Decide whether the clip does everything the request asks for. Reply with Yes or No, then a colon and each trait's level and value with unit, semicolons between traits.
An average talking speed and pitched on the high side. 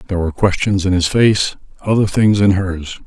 No: average, 175 wpm; very low, 95 Hz